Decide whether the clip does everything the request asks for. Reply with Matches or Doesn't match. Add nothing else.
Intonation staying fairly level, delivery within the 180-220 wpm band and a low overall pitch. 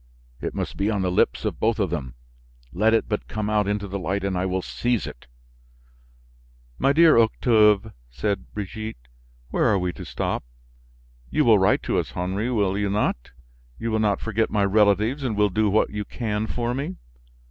Matches